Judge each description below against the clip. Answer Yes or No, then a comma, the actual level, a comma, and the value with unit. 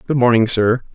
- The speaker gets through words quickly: No, average, 190 wpm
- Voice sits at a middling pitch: No, low, 120 Hz